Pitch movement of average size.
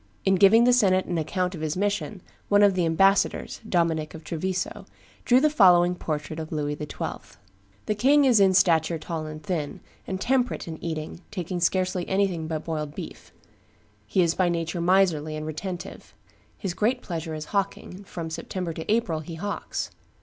Yes: average, 3.5 semitones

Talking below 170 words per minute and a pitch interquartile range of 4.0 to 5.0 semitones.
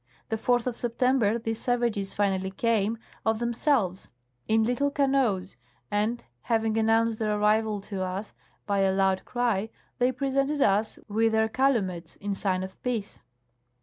No: average, 150 wpm; average, 3.2 semitones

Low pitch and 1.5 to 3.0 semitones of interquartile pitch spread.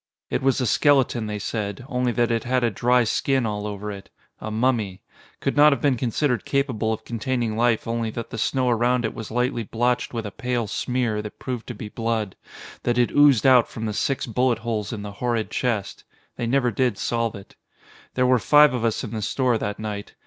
Yes: low, 120 Hz; narrow, 2.6 semitones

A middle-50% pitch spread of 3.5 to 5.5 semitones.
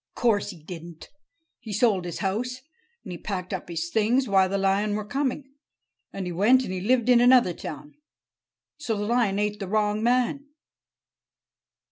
Yes: average, 4.5 semitones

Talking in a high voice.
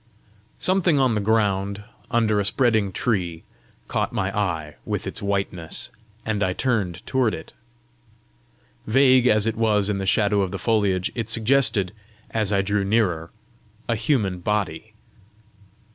No: low, 105 Hz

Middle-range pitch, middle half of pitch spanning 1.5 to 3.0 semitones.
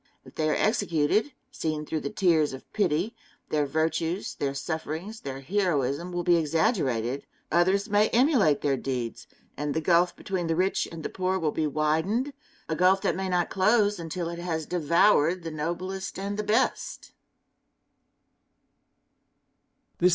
No: medium, 170 Hz; average, 3.9 semitones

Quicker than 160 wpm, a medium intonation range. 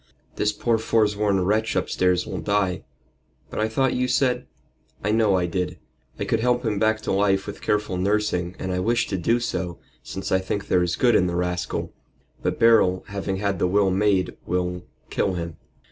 Yes: average, 195 wpm; average, 3.1 semitones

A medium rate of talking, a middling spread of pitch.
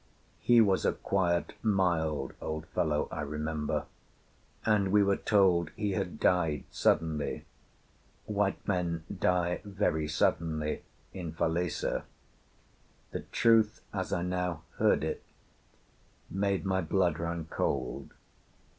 No: slow, 115 wpm; average, 3.6 semitones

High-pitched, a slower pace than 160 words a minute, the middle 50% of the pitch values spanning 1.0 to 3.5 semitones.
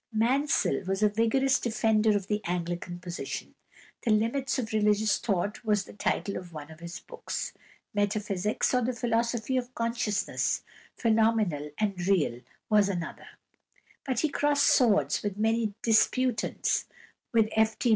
Yes: high, 215 Hz; average, 145 wpm; average, 3.0 semitones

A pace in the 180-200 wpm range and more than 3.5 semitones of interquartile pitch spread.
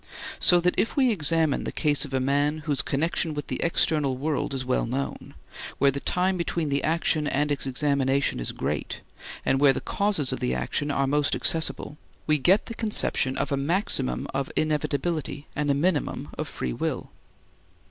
No: average, 185 wpm; average, 3.0 semitones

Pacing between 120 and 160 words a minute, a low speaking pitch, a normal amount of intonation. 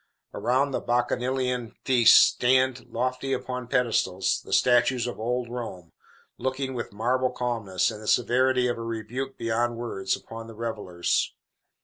No: average, 140 wpm; low, 120 Hz; narrow, 2.0 semitones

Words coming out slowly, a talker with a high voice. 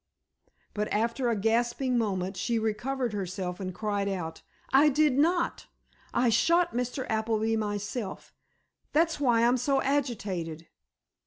Yes: slow, 130 wpm; high, 230 Hz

